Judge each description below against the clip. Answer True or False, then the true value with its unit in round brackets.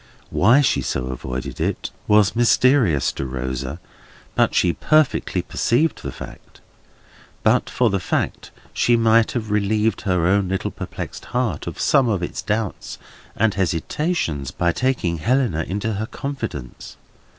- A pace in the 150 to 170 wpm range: False (140 wpm)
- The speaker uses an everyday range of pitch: False (6.3 semitones)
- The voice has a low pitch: True (105 Hz)